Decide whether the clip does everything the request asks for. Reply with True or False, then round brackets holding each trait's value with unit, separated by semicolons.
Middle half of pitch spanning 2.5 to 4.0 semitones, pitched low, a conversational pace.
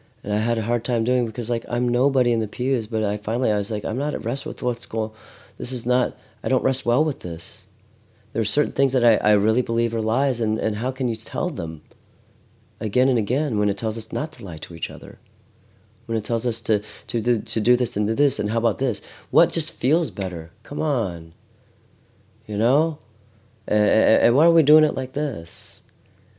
False (2.8 semitones; 115 Hz; 230 wpm)